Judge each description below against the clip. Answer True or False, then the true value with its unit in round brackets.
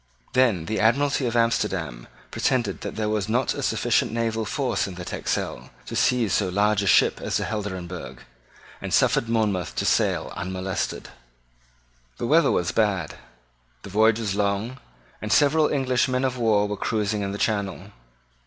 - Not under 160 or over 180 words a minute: True (165 wpm)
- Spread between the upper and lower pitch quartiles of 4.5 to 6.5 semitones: False (3.3 semitones)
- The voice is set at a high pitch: False (110 Hz)